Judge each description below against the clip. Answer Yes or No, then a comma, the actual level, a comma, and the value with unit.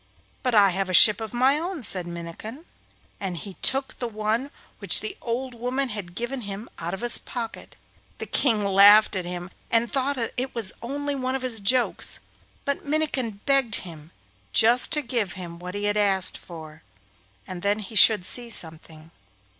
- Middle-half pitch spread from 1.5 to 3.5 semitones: No, average, 5.2 semitones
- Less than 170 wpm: No, average, 185 wpm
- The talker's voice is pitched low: No, high, 220 Hz